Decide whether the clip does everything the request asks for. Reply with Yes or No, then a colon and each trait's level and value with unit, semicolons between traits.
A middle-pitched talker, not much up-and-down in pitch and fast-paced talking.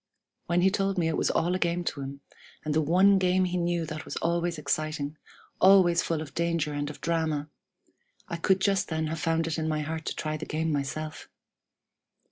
Yes: medium, 165 Hz; narrow, 2.2 semitones; fast, 210 wpm